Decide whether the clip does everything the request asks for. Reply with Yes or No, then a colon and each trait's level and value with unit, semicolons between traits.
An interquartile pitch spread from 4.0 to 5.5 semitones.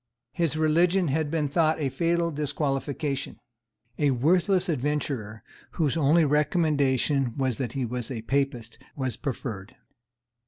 No: average, 3.5 semitones